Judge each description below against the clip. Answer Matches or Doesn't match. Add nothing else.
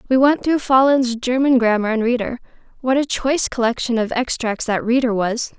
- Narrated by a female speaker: Matches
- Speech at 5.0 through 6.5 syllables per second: Matches